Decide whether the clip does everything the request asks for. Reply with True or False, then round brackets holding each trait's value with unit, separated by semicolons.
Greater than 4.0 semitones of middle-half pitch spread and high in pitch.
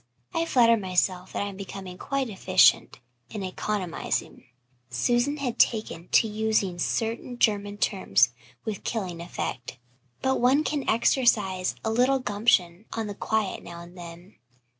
True (4.4 semitones; 205 Hz)